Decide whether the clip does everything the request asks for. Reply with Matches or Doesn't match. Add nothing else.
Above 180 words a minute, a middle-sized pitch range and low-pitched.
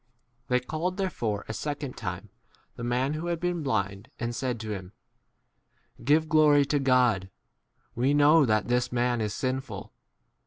Doesn't match